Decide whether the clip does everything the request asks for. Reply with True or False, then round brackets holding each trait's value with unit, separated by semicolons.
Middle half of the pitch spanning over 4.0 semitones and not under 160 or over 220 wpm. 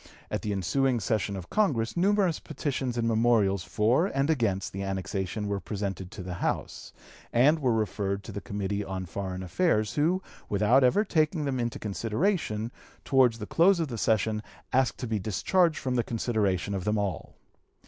True (5.4 semitones; 175 wpm)